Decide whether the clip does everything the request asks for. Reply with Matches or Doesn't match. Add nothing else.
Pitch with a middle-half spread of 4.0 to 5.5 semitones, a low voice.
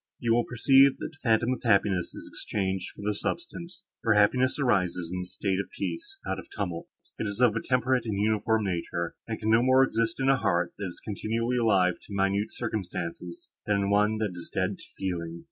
Matches